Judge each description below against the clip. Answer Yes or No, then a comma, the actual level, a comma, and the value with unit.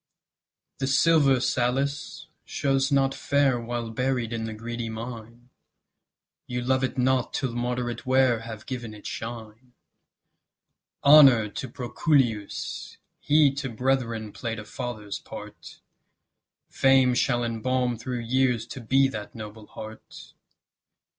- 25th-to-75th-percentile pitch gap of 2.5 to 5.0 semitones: Yes, average, 2.8 semitones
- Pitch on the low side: Yes, low, 120 Hz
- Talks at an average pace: No, slow, 120 wpm